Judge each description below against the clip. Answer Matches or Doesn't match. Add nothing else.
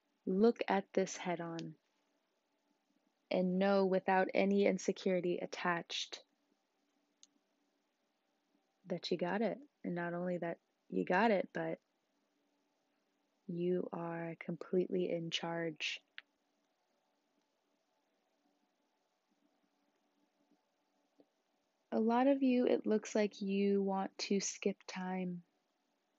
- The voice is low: Doesn't match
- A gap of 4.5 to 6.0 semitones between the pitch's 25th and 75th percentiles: Doesn't match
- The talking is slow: Matches